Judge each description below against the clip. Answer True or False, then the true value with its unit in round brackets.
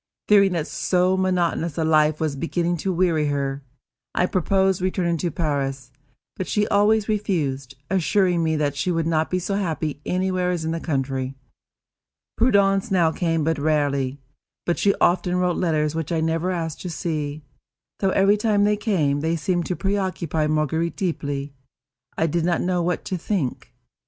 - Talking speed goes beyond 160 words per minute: True (170 wpm)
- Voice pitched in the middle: True (170 Hz)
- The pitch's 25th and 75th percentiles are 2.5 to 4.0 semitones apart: True (3.4 semitones)